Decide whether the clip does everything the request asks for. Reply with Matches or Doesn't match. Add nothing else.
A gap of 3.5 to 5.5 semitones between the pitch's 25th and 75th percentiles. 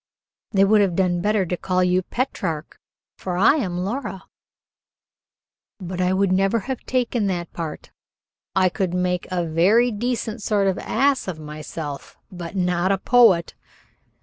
Doesn't match